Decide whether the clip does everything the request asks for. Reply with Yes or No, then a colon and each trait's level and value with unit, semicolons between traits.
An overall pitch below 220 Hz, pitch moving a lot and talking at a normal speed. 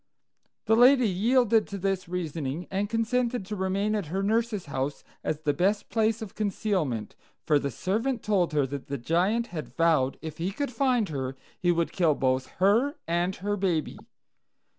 Yes: high, 190 Hz; wide, 5.7 semitones; average, 175 wpm